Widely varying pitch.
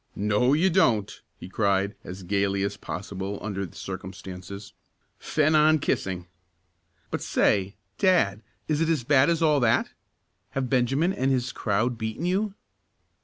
Yes: wide, 7.3 semitones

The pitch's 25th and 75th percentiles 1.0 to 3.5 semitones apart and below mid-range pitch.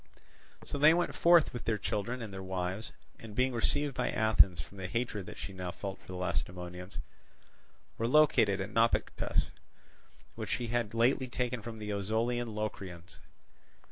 No: average, 4.0 semitones; low, 110 Hz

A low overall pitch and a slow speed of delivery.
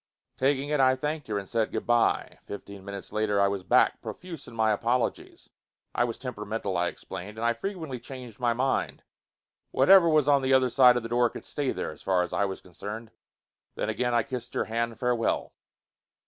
No: low, 120 Hz; fast, 205 wpm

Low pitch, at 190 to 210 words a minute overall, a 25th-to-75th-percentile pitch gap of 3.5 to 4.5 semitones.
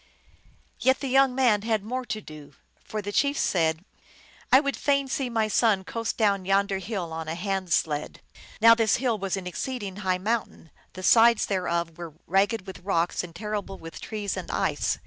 No: high, 205 Hz; average, 195 wpm; average, 4.1 semitones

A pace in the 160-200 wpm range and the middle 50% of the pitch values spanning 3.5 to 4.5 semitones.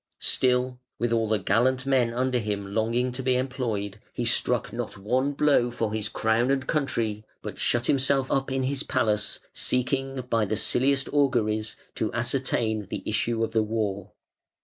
No: average, 170 wpm; average, 3.1 semitones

